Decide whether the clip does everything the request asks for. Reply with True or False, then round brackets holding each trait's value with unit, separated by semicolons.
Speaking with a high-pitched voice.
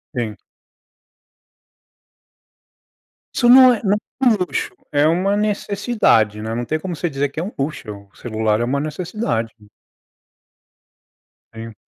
False (155 Hz)